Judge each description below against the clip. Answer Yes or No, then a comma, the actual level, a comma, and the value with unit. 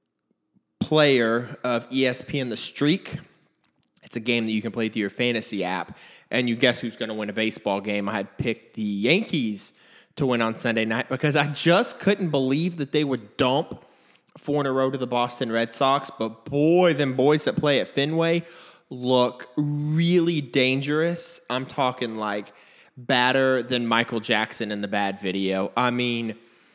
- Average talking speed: Yes, average, 175 wpm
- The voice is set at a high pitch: No, low, 125 Hz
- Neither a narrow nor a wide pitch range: Yes, average, 4.4 semitones